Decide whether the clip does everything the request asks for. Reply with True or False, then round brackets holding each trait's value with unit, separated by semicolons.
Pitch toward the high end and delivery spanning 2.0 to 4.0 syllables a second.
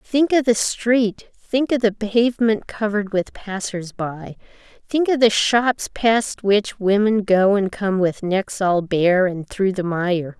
True (205 Hz; 3.7 syllables/s)